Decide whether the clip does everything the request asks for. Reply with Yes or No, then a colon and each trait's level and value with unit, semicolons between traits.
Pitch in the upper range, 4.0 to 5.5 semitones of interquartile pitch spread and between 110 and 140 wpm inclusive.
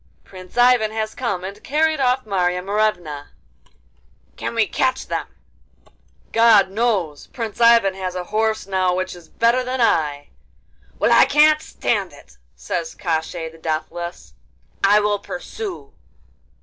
Yes: high, 200 Hz; average, 4.8 semitones; slow, 135 wpm